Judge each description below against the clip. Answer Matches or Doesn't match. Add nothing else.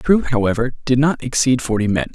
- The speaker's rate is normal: Doesn't match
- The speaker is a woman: Doesn't match